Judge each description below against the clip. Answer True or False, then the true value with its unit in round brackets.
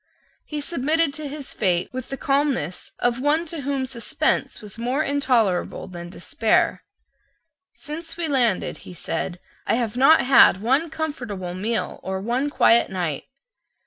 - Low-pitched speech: False (255 Hz)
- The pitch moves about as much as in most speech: False (6.6 semitones)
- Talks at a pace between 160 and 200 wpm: False (145 wpm)